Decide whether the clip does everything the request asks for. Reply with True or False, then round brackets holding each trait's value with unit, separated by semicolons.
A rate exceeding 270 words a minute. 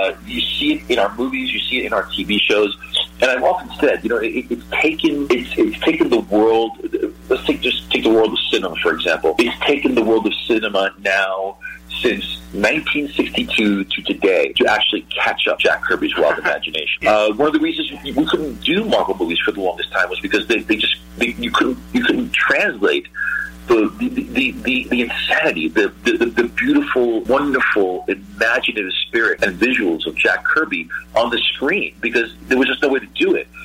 False (200 wpm)